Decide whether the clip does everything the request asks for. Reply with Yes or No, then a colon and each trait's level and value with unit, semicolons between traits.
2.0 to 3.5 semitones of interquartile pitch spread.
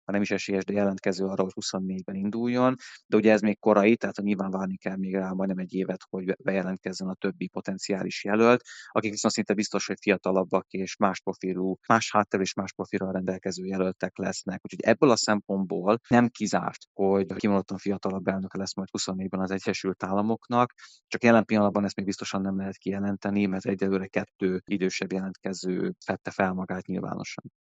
No: narrow, 1.5 semitones